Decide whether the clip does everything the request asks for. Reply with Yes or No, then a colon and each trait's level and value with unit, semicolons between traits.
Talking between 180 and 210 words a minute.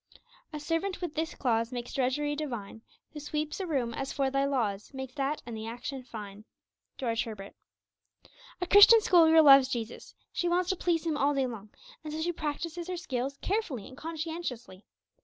Yes: average, 185 wpm